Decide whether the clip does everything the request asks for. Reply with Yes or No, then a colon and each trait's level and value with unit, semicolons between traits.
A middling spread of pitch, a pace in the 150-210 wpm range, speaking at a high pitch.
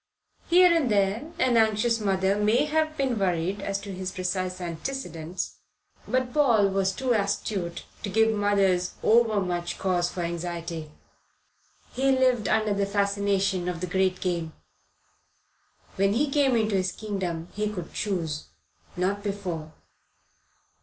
No: average, 3.6 semitones; average, 140 wpm; high, 200 Hz